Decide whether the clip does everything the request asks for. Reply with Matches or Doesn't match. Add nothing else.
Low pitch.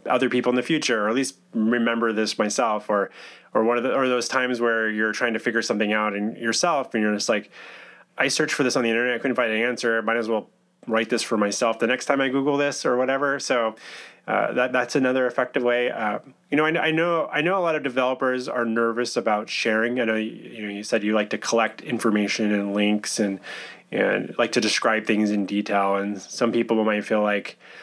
Matches